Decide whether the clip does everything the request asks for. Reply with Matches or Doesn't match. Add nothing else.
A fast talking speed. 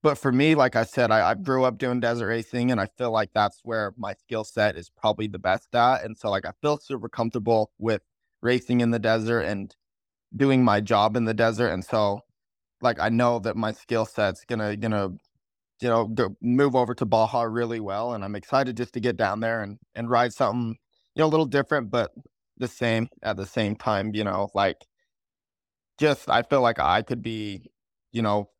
Matches